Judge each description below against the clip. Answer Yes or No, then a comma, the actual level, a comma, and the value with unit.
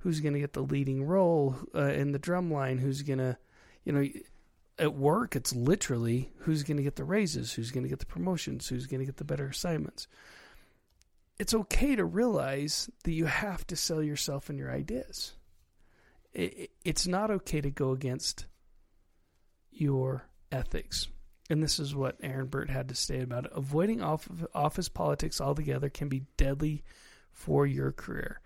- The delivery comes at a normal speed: Yes, average, 170 wpm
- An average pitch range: Yes, average, 3.6 semitones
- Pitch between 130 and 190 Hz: Yes, medium, 140 Hz